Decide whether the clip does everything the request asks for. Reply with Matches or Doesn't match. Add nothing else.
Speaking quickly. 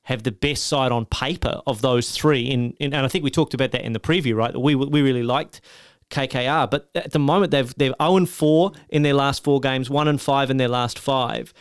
Matches